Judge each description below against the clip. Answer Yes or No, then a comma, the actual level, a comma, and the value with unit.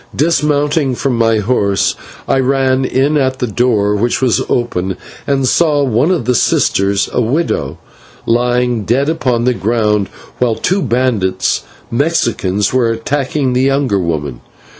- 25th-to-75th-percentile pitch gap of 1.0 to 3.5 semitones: No, average, 4.2 semitones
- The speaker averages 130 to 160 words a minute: Yes, average, 140 wpm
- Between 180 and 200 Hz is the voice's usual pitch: No, low, 125 Hz